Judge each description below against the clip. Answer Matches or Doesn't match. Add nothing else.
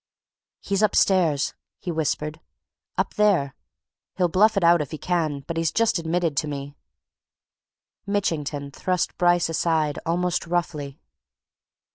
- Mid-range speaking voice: Matches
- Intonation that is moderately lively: Matches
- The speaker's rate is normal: Doesn't match